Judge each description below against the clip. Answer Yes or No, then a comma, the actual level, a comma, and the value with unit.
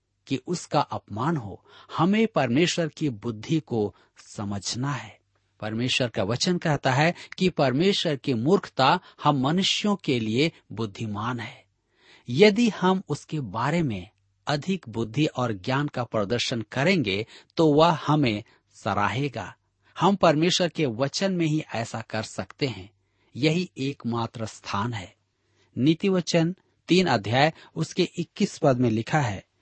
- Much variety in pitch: Yes, wide, 6.6 semitones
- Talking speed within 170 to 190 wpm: No, average, 135 wpm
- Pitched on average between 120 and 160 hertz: Yes, low, 135 Hz